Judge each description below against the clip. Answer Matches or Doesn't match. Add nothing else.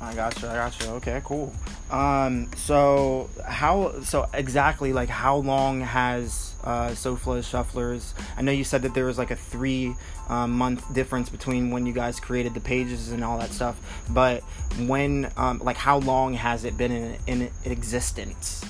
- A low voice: Matches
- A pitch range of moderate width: Doesn't match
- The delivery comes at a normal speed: Matches